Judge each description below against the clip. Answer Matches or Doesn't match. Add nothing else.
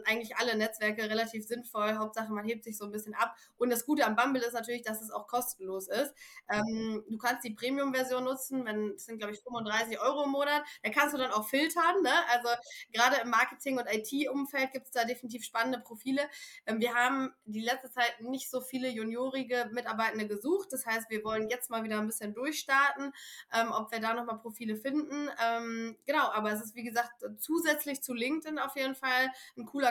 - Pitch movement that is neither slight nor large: Matches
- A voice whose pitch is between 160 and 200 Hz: Doesn't match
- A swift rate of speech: Matches